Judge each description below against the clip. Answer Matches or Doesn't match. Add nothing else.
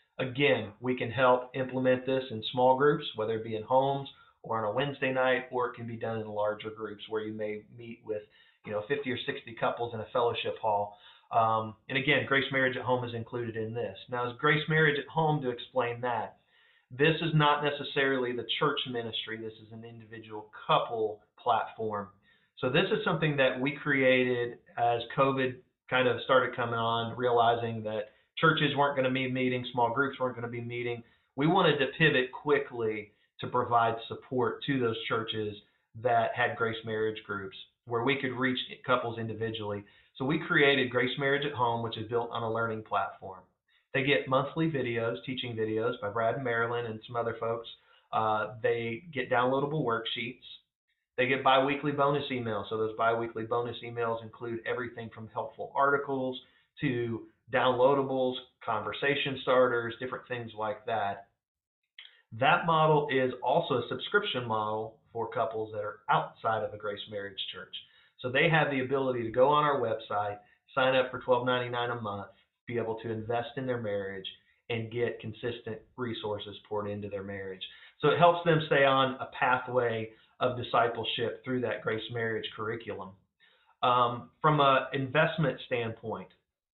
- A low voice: Matches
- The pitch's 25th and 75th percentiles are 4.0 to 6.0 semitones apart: Doesn't match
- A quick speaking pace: Doesn't match